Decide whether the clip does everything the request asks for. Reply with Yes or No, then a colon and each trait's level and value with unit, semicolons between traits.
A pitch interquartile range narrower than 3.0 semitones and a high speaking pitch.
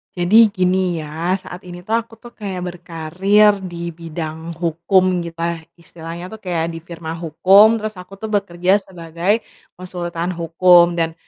No: narrow, 2.4 semitones; medium, 175 Hz